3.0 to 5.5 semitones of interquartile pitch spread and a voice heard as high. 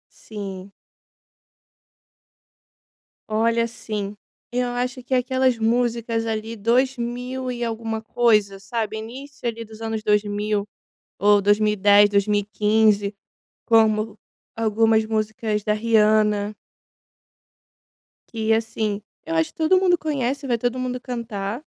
No: narrow, 2.4 semitones; high, 220 Hz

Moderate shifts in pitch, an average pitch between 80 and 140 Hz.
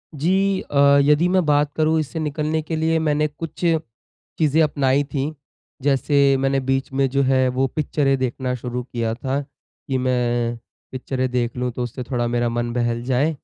Yes: average, 3.3 semitones; low, 135 Hz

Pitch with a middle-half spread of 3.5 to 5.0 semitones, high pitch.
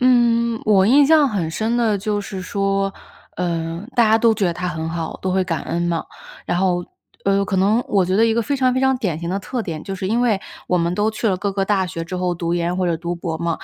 Yes: average, 4.1 semitones; high, 195 Hz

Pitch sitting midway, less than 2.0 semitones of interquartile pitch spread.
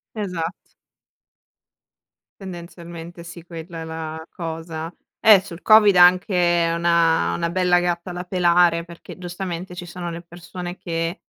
Yes: medium, 175 Hz; narrow, 1.2 semitones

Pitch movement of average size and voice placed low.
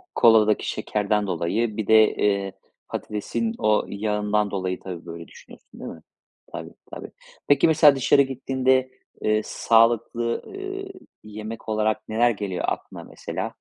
Yes: average, 3.7 semitones; low, 110 Hz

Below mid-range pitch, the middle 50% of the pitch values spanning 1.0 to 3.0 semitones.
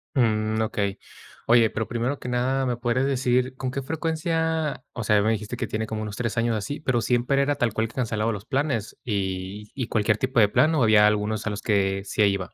No: low, 115 Hz; average, 3.6 semitones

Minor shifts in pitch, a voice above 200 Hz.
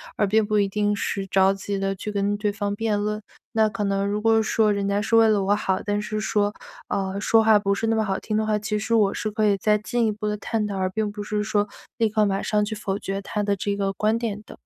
Yes: narrow, 1.3 semitones; high, 210 Hz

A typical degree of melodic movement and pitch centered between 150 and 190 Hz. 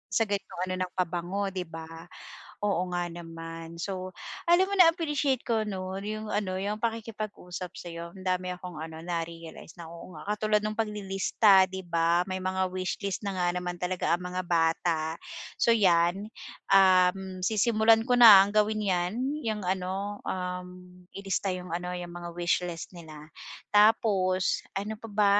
Yes: average, 3.1 semitones; medium, 185 Hz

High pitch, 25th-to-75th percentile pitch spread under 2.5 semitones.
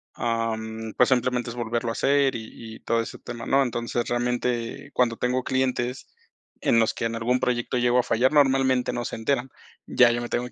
No: low, 120 Hz; narrow, 1.7 semitones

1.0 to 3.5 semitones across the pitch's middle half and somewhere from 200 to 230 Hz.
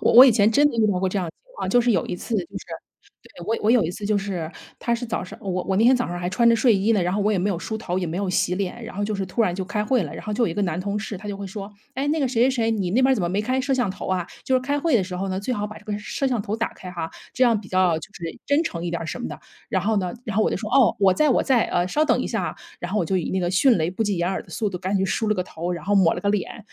No: average, 4.0 semitones; high, 205 Hz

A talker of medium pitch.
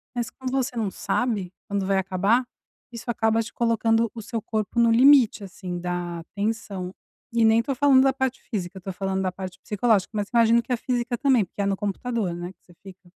No: high, 220 Hz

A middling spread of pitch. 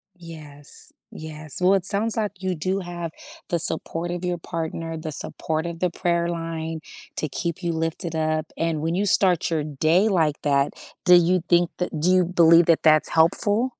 No: narrow, 2.1 semitones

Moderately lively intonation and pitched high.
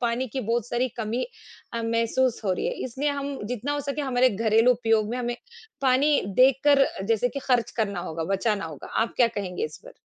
Yes: average, 3.0 semitones; high, 240 Hz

